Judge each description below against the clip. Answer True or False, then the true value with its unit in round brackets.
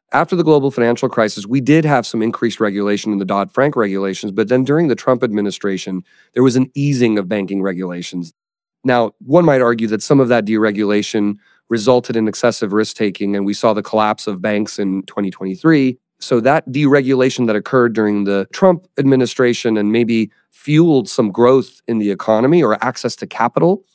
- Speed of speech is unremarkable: True (185 wpm)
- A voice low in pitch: True (115 Hz)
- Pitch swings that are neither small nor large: True (4.2 semitones)